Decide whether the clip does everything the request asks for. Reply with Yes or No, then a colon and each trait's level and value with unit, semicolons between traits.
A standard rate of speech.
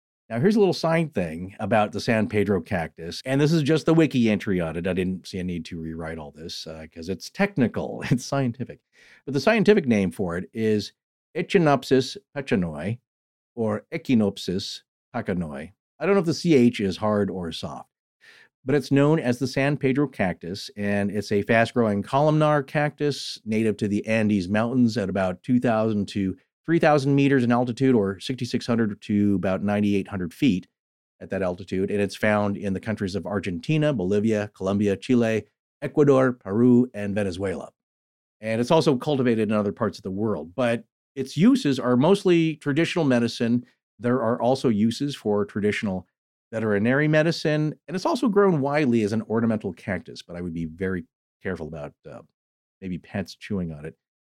Yes: average, 175 wpm